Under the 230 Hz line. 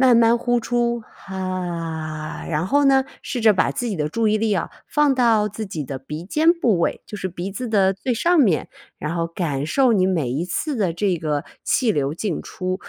Yes: high, 190 Hz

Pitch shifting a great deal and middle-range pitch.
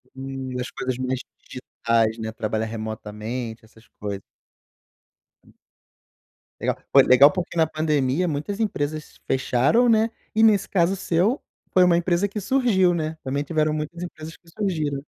Yes: wide, 6.1 semitones; medium, 150 Hz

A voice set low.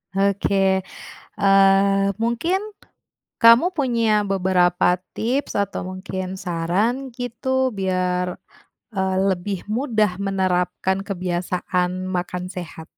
No: high, 195 Hz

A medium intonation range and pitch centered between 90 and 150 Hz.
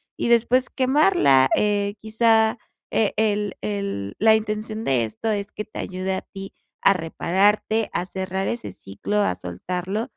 No: average, 3.0 semitones; high, 205 Hz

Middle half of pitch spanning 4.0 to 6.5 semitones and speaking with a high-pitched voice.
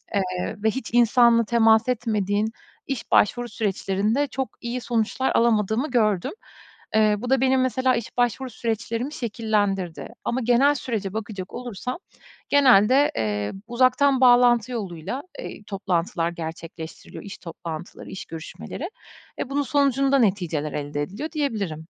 Yes: average, 4.6 semitones; high, 225 Hz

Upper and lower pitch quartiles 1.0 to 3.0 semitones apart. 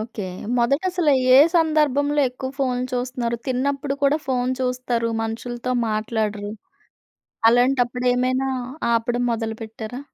Yes: average, 2.7 semitones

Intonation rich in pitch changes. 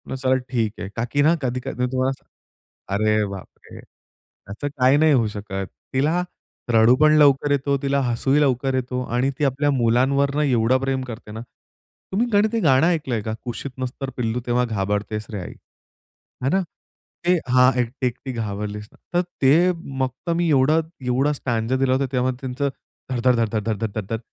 No: average, 3.5 semitones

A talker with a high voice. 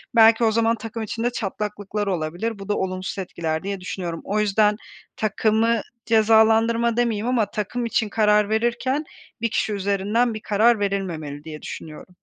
Yes: high, 210 Hz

